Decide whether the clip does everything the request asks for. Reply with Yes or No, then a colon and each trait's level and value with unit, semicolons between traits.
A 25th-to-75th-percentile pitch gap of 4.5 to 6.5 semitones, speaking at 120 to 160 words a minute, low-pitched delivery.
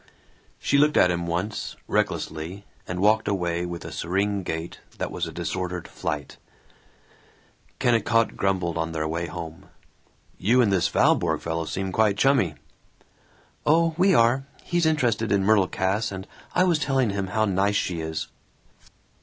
Yes: average, 5.0 semitones; average, 155 wpm; very low, 95 Hz